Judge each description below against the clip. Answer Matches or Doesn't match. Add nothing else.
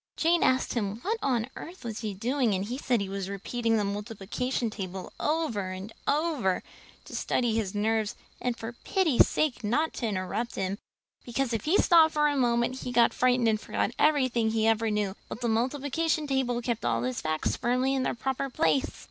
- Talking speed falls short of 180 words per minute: Doesn't match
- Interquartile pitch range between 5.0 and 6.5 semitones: Doesn't match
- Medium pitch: Doesn't match